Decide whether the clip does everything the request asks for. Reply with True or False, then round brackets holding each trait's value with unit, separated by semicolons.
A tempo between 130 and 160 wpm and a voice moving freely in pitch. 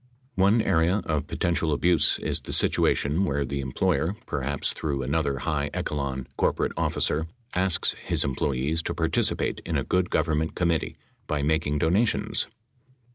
False (150 wpm; 3.4 semitones)